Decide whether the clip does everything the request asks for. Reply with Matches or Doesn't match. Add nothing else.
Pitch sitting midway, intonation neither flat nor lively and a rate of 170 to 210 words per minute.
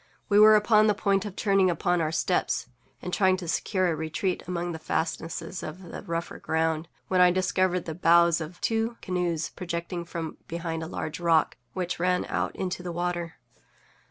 Doesn't match